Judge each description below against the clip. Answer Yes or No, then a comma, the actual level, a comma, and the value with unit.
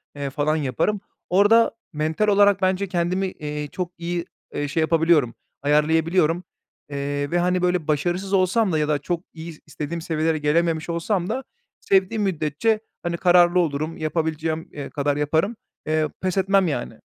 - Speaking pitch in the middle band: Yes, medium, 165 Hz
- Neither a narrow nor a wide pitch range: Yes, average, 3.4 semitones